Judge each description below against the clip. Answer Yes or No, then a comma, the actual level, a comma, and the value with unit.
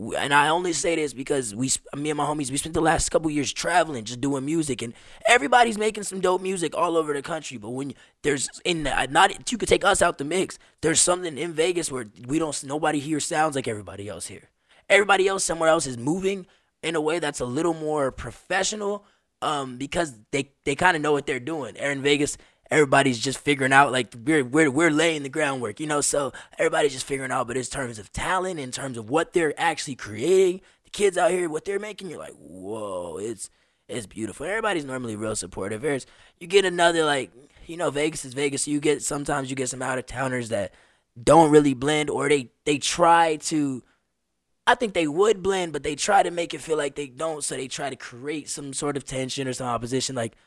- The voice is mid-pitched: Yes, medium, 150 Hz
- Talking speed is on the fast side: Yes, fast, 225 wpm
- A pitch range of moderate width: Yes, average, 4.0 semitones